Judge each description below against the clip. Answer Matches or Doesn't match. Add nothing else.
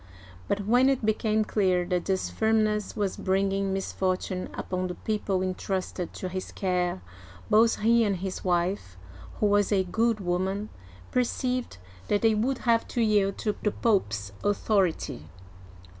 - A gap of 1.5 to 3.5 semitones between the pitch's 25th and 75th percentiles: Matches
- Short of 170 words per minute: Matches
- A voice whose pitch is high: Matches